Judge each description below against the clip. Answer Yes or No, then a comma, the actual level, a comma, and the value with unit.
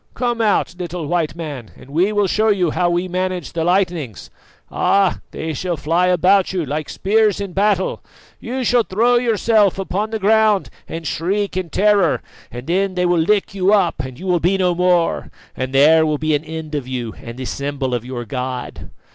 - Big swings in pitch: No, average, 4.5 semitones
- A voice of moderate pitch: Yes, medium, 180 Hz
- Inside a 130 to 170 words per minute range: No, average, 195 wpm